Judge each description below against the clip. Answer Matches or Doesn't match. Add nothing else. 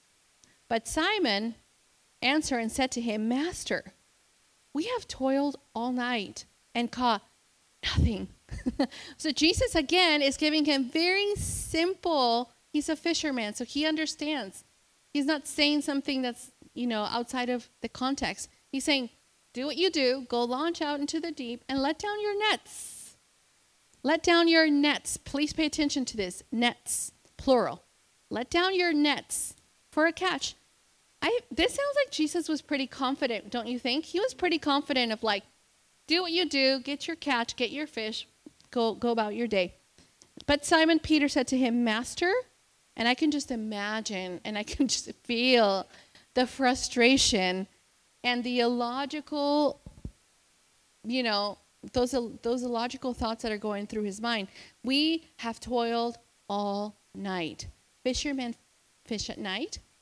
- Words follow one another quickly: Doesn't match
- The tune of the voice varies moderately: Matches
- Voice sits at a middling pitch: Doesn't match